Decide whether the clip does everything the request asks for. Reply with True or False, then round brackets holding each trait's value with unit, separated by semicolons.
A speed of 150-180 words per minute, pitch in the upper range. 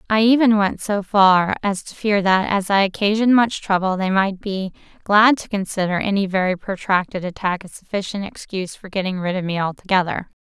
False (190 wpm; 195 Hz)